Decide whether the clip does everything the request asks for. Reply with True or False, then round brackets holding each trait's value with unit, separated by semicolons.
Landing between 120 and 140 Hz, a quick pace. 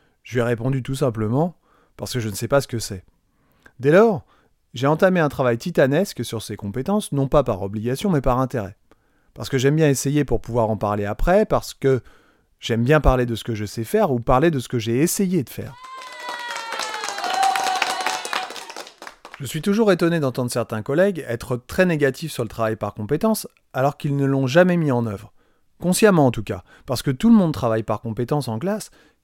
False (135 Hz; 205 wpm)